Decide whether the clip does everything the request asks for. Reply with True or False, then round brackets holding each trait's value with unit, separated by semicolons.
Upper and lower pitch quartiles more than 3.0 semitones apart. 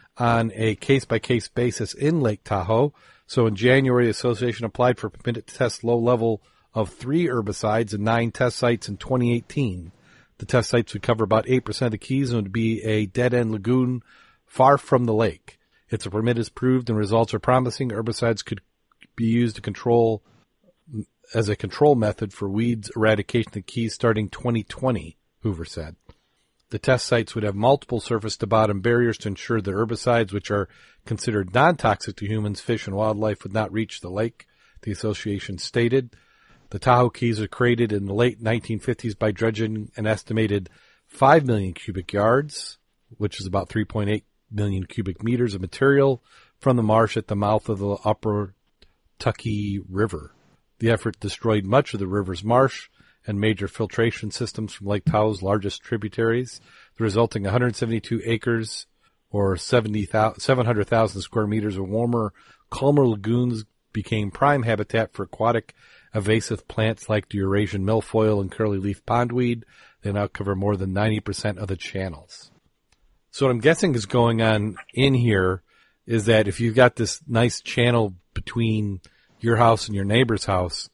False (2.5 semitones)